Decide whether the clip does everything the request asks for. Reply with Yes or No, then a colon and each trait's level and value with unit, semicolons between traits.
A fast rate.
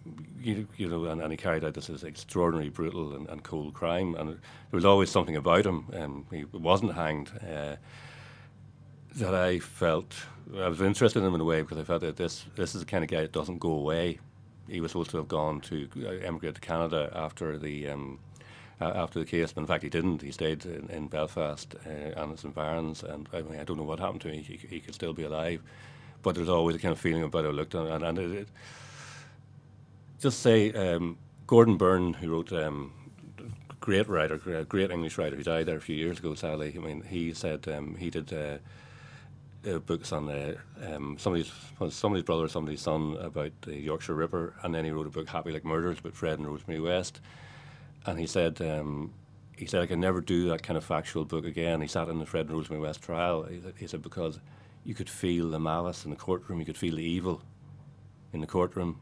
Yes: fast, 230 wpm